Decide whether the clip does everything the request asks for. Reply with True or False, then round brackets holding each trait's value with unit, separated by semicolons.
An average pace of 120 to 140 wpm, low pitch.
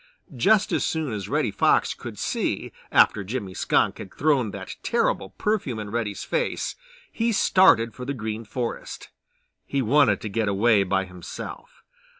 False (155 wpm; 115 Hz)